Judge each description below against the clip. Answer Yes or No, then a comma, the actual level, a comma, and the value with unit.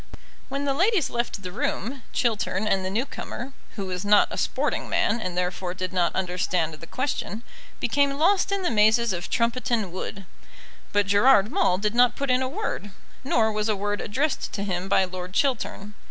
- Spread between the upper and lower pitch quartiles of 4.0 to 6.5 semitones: Yes, wide, 5.5 semitones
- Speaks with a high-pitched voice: Yes, high, 210 Hz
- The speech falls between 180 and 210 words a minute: Yes, average, 190 wpm